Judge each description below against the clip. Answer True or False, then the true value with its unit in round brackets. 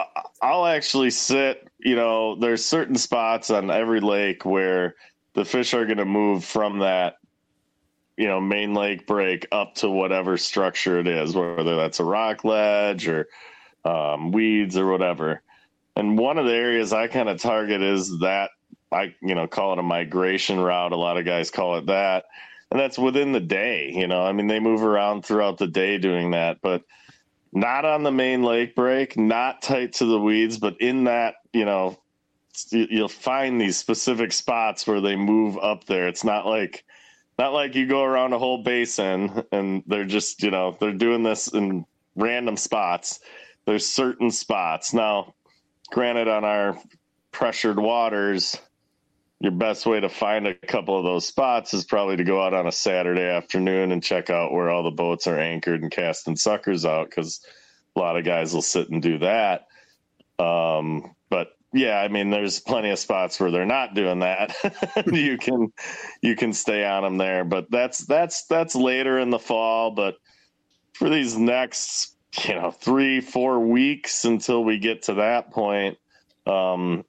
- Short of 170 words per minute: False (180 wpm)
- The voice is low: True (105 Hz)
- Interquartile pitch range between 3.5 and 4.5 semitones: True (4.2 semitones)